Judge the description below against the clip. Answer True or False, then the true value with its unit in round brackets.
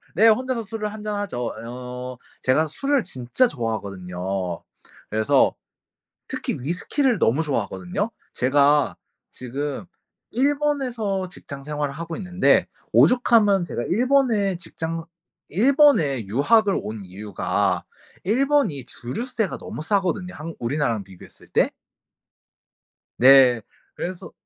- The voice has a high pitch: False (170 Hz)